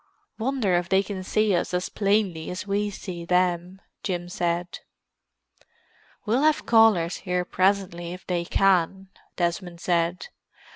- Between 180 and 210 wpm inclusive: No, slow, 135 wpm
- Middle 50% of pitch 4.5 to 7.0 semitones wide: No, narrow, 2.4 semitones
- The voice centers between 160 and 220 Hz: Yes, medium, 185 Hz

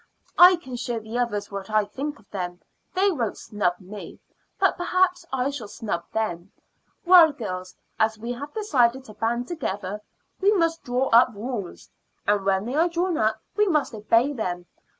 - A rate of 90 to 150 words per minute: No, average, 175 wpm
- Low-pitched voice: No, high, 235 Hz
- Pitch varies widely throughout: Yes, wide, 6.6 semitones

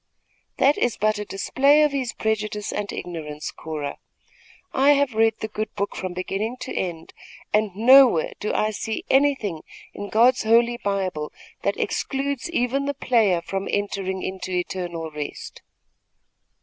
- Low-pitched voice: No, high, 210 Hz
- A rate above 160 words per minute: No, average, 150 wpm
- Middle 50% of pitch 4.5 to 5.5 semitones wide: Yes, average, 5.1 semitones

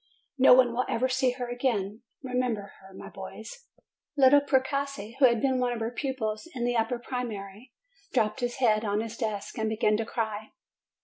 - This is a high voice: Yes, high, 240 Hz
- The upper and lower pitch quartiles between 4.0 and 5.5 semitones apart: No, average, 3.0 semitones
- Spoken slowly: No, average, 190 wpm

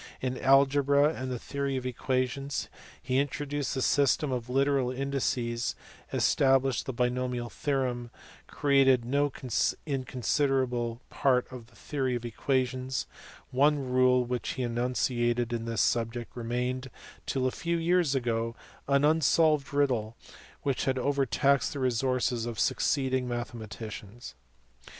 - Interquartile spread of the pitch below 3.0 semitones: Yes, narrow, 2.4 semitones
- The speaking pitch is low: Yes, low, 130 Hz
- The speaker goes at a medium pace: No, slow, 130 wpm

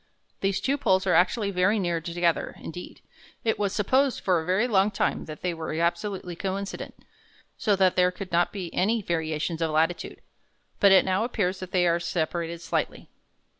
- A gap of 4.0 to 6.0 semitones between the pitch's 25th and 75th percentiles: No, average, 2.7 semitones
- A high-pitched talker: No, medium, 180 Hz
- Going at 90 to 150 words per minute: No, average, 180 wpm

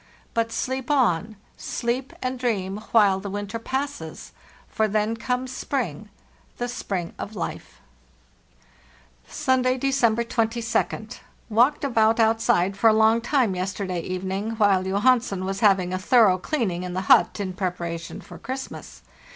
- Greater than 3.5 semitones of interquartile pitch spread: Yes, average, 4.2 semitones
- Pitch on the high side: Yes, high, 220 Hz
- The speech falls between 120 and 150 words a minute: Yes, slow, 135 wpm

